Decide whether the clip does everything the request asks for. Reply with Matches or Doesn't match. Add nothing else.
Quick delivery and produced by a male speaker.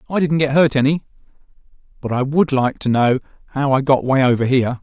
Matches